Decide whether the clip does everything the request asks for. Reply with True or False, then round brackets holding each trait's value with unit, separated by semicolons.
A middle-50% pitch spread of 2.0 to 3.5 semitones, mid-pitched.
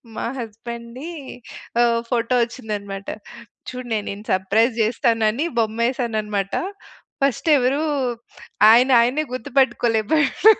False (2.8 semitones; 235 Hz)